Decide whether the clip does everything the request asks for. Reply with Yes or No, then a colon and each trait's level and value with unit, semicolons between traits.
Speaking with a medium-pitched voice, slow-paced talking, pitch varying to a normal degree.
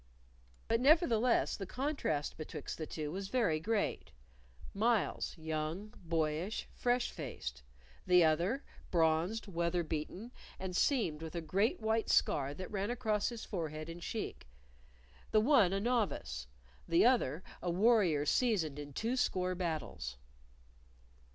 No: medium, 180 Hz; slow, 130 wpm; wide, 6.2 semitones